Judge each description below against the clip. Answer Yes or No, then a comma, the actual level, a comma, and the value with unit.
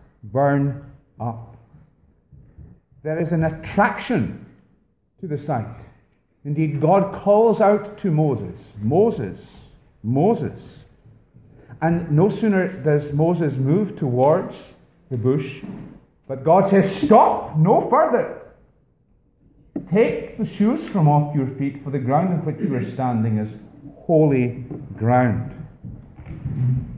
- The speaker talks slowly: Yes, slow, 110 wpm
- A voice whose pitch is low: No, medium, 145 Hz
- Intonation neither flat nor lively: No, wide, 6.2 semitones